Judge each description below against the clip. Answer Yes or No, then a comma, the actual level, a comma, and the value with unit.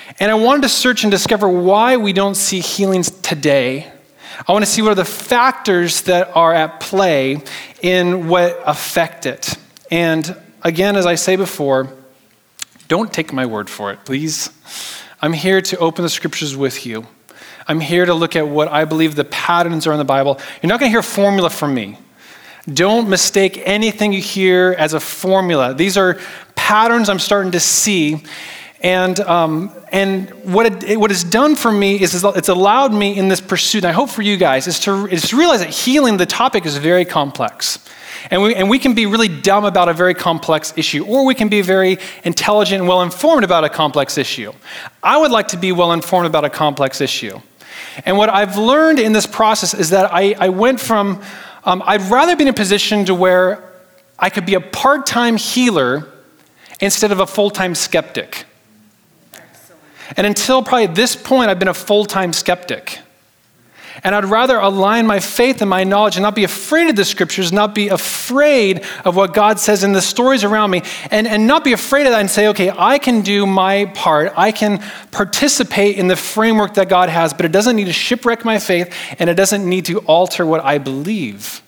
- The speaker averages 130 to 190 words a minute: No, average, 200 wpm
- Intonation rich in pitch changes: No, average, 3.7 semitones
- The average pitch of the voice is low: No, high, 190 Hz